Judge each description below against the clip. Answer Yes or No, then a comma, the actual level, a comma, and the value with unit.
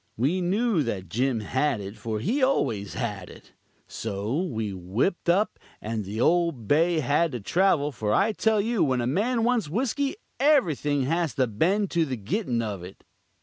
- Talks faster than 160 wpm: Yes, average, 180 wpm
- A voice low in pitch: No, medium, 145 Hz